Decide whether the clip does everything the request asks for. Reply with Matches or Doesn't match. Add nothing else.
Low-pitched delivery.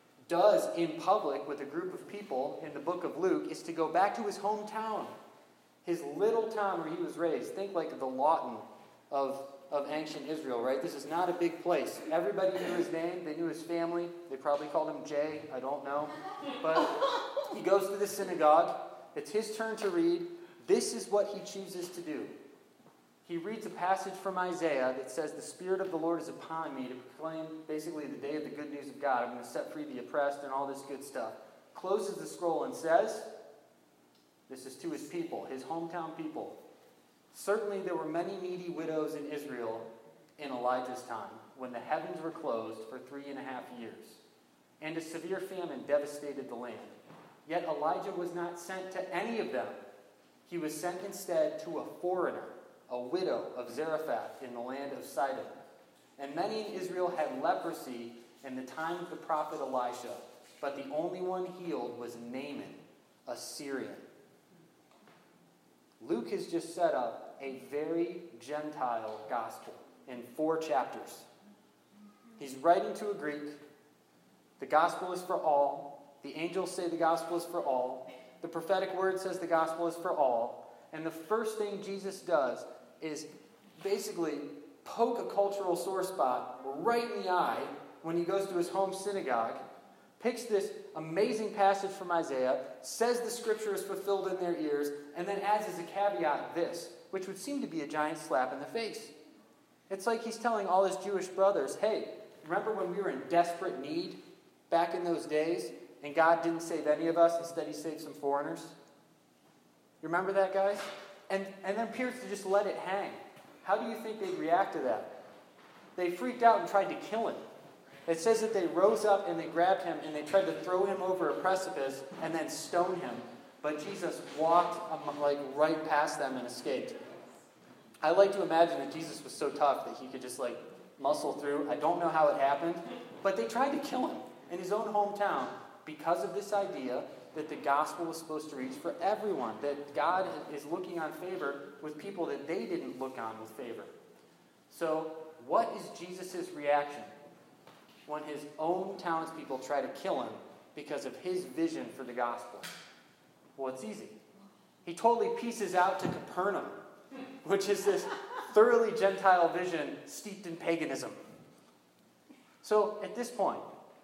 Doesn't match